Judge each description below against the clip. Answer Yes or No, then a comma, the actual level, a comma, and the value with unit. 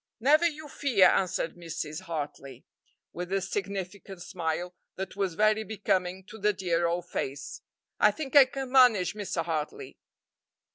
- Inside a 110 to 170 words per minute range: Yes, average, 145 wpm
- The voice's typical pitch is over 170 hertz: Yes, high, 190 Hz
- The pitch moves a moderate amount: Yes, average, 3.9 semitones